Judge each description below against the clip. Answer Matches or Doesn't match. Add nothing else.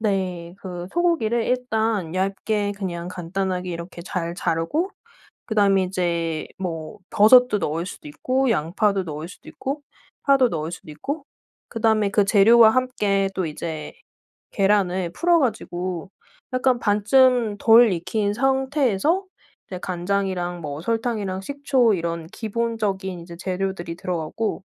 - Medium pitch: Doesn't match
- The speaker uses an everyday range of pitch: Matches